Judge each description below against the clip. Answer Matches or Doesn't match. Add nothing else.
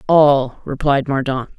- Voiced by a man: Matches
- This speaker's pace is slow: Matches